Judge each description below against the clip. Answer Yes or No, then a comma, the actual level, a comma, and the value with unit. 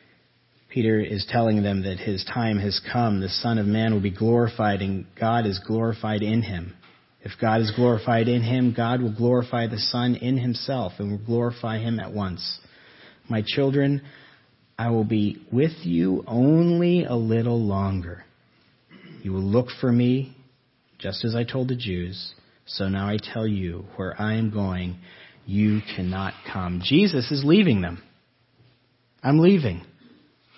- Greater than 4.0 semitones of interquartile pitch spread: No, average, 3.7 semitones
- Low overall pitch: Yes, low, 110 Hz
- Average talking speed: Yes, average, 160 wpm